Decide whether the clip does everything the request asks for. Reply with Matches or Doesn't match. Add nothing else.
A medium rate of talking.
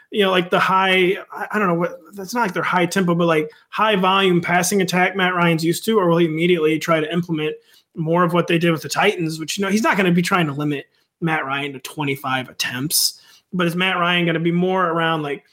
Doesn't match